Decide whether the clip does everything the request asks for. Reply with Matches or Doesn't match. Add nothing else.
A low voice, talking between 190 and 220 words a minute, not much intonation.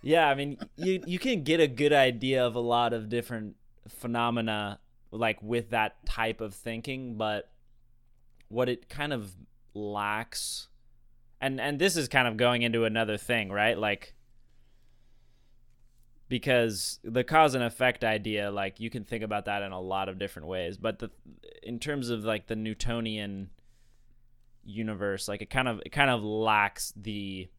Doesn't match